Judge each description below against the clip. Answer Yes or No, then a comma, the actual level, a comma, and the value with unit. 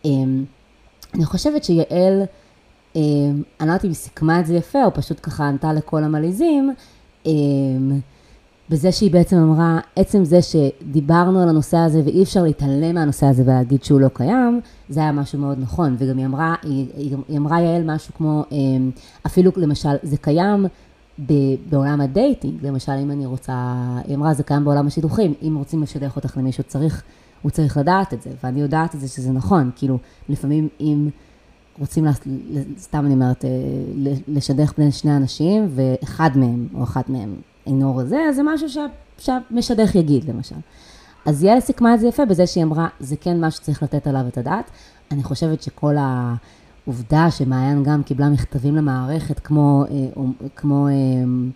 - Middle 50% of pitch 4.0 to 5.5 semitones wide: No, average, 3.3 semitones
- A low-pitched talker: No, medium, 145 Hz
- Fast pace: Yes, fast, 165 wpm